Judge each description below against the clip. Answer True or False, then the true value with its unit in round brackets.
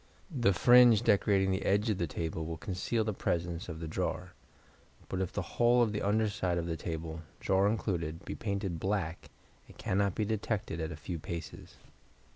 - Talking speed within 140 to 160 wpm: False (190 wpm)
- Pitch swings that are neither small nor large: True (4.0 semitones)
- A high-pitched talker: False (95 Hz)